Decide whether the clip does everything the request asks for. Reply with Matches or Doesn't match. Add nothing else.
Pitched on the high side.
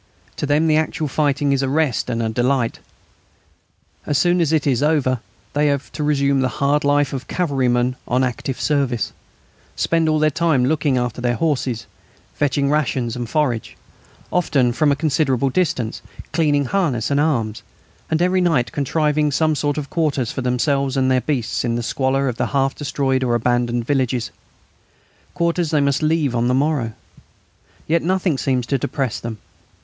Doesn't match